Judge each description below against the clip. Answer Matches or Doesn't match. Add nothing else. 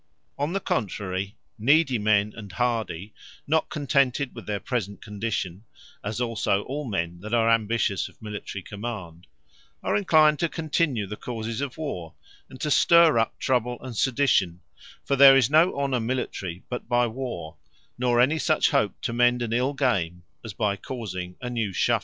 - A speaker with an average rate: Matches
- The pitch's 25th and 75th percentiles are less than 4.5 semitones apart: Doesn't match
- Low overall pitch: Matches